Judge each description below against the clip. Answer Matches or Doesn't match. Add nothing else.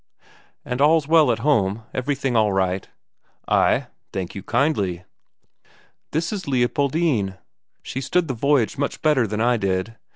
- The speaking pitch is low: Matches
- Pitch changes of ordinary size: Doesn't match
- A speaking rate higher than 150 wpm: Doesn't match